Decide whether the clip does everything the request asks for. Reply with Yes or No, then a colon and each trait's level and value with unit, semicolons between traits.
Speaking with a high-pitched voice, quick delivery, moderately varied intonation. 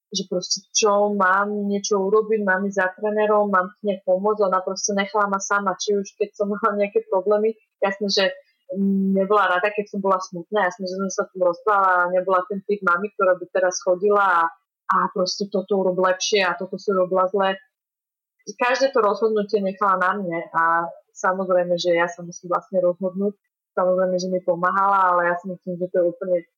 No: high, 195 Hz; fast, 195 wpm; narrow, 2.0 semitones